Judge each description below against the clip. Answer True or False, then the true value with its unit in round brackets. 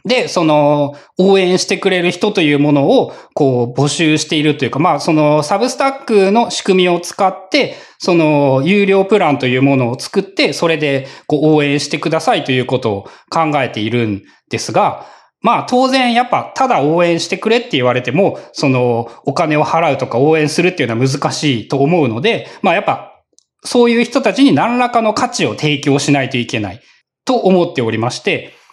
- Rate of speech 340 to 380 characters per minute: True (370 characters per minute)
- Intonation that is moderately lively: False (6.0 semitones)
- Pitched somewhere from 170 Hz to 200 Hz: False (155 Hz)